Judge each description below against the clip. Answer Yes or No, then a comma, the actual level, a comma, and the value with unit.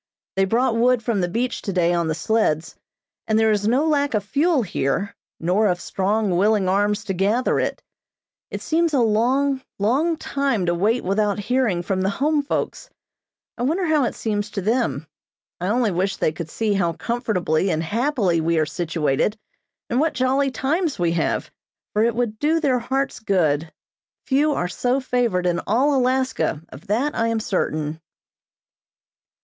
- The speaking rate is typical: Yes, average, 175 wpm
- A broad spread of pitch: Yes, wide, 6.1 semitones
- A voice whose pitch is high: Yes, high, 220 Hz